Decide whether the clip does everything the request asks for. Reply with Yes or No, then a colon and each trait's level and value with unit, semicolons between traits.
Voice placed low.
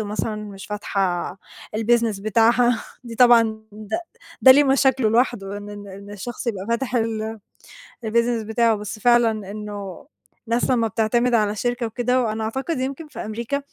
No: high, 225 Hz